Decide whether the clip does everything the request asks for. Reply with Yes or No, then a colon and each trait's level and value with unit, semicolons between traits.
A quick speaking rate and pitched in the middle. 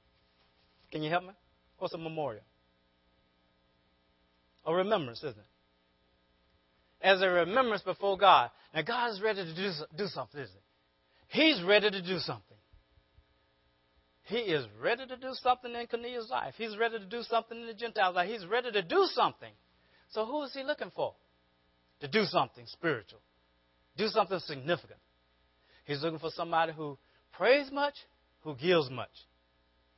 No: average, 155 wpm; medium, 155 Hz